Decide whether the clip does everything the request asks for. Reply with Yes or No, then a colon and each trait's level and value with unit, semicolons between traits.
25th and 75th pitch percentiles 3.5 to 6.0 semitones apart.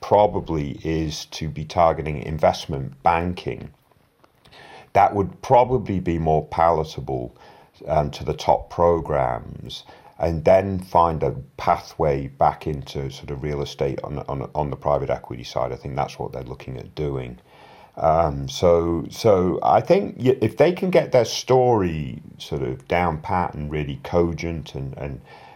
No: average, 2.8 semitones